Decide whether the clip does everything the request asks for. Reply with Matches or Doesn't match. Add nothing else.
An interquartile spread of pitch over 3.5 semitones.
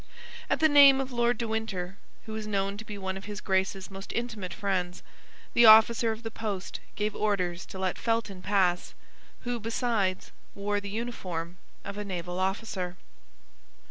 Doesn't match